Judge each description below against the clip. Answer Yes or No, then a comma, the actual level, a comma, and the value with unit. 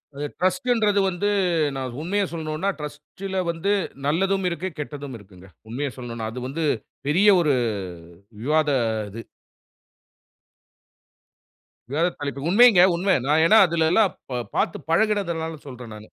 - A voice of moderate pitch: Yes, medium, 160 Hz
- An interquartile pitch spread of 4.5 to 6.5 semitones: Yes, average, 5.2 semitones